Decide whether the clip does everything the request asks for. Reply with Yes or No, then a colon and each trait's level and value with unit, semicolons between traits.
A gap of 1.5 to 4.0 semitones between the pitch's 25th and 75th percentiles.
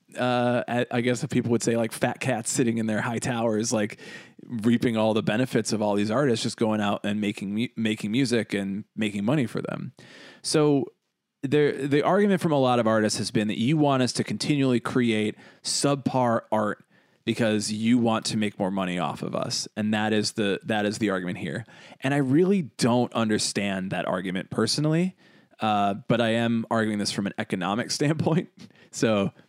Yes: average, 3.2 semitones